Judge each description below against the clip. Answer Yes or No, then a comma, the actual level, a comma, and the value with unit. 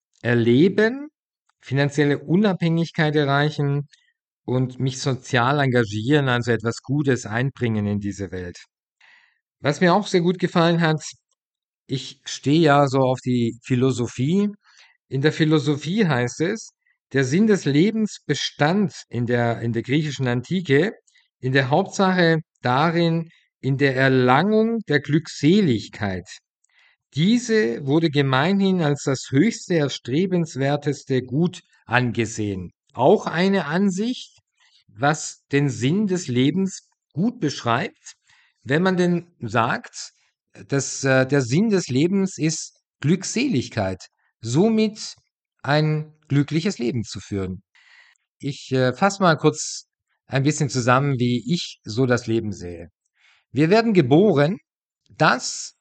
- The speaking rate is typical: No, slow, 115 wpm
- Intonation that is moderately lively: No, wide, 5.8 semitones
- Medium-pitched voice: Yes, medium, 145 Hz